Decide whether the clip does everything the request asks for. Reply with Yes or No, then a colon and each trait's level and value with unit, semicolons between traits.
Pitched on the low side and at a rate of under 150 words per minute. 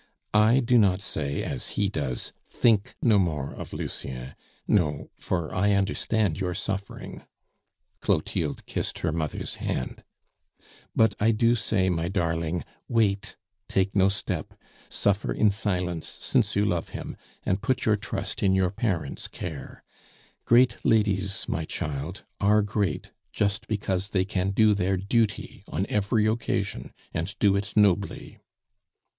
Yes: low, 100 Hz; average, 140 wpm